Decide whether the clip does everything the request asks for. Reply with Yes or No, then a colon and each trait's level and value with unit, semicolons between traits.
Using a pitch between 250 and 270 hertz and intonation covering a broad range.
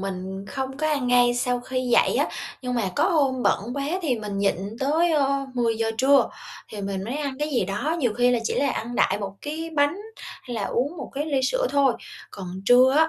No: very high, 255 Hz; average, 4.2 semitones